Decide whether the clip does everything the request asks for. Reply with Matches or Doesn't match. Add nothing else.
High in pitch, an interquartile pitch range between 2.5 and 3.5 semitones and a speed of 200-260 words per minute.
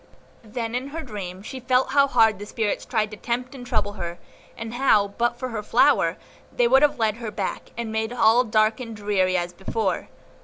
Matches